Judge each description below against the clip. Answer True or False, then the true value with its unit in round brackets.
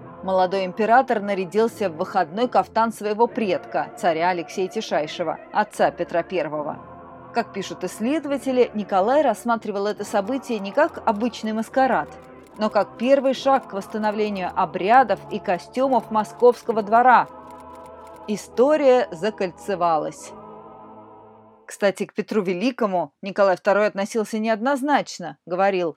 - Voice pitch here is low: False (210 Hz)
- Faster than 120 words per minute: False (110 wpm)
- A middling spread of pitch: True (4.0 semitones)